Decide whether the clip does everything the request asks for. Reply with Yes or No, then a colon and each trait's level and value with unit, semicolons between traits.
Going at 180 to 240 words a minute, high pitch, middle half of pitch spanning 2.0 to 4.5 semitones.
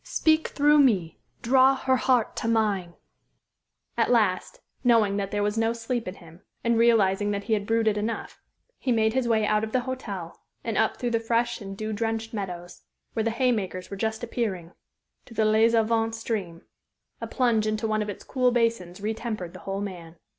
Yes: average, 190 wpm; high, 220 Hz; narrow, 2.6 semitones